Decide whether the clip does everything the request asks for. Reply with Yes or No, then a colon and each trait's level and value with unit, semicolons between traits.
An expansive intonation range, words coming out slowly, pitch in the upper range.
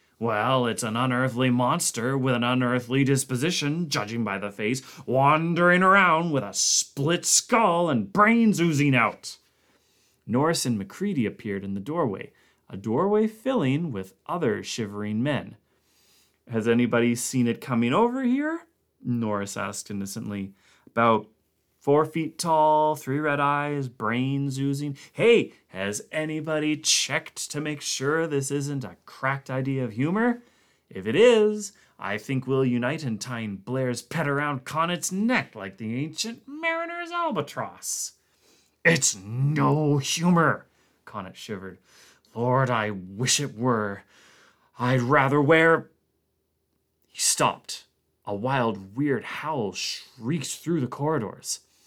No: wide, 5.7 semitones; slow, 130 wpm; low, 135 Hz